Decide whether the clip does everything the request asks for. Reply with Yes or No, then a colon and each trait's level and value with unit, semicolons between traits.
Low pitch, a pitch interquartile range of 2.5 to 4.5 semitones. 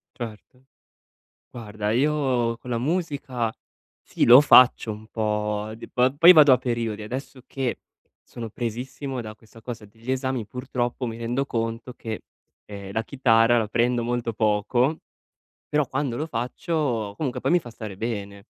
Yes: low, 120 Hz; average, 2.9 semitones